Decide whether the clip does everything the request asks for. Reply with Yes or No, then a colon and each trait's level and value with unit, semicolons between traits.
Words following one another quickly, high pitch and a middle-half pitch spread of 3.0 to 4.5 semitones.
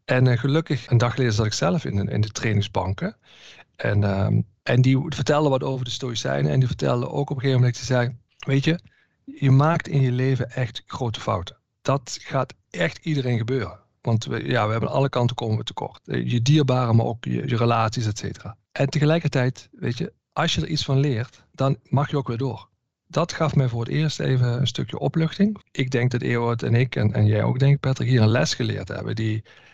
No: fast, 225 wpm; low, 125 Hz; average, 3.6 semitones